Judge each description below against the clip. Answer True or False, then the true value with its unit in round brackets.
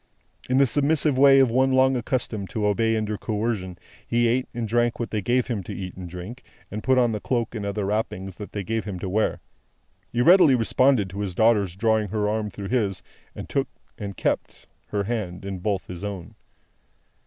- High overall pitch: False (110 Hz)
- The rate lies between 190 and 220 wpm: True (205 wpm)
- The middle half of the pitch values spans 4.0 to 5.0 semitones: False (3.5 semitones)